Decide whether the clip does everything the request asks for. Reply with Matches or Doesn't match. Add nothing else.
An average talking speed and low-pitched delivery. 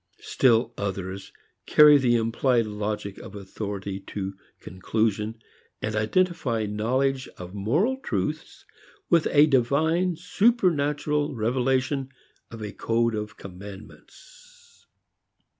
Doesn't match